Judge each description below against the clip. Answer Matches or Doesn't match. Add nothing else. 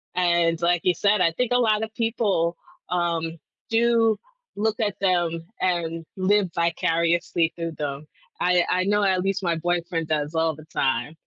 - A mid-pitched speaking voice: Matches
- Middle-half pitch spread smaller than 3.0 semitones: Doesn't match